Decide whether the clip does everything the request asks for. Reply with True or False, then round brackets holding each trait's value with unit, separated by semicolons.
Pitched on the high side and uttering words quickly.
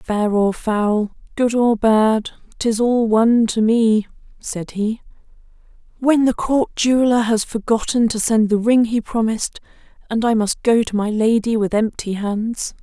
False (225 Hz; 165 wpm)